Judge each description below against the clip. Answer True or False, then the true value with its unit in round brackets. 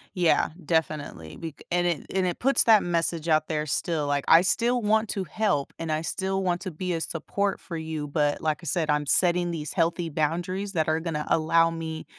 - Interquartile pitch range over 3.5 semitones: False (2.7 semitones)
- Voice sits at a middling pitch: True (165 Hz)